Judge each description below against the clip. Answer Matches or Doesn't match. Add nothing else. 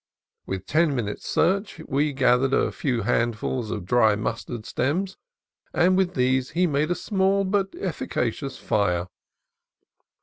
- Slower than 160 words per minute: Matches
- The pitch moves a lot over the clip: Matches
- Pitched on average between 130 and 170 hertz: Matches